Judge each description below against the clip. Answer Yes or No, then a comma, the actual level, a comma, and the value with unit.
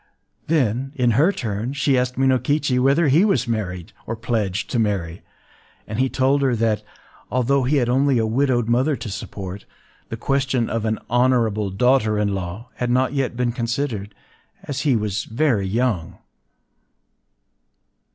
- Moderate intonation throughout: Yes, average, 3.8 semitones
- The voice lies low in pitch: Yes, low, 120 Hz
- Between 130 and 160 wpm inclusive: Yes, average, 155 wpm